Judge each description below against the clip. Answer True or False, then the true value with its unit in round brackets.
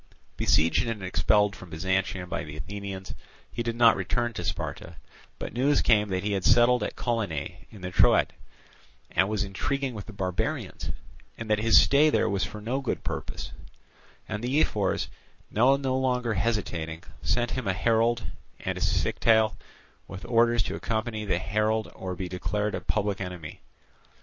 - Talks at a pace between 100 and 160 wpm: False (170 wpm)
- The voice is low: True (105 Hz)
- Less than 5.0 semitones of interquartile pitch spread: True (3.9 semitones)